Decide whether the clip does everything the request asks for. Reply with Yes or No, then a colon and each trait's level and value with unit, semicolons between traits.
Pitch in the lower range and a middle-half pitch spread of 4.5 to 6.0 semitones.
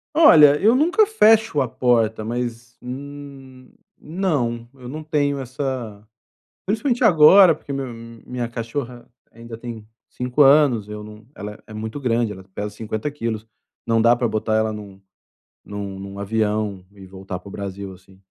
Yes: low, 120 Hz; average, 5.0 semitones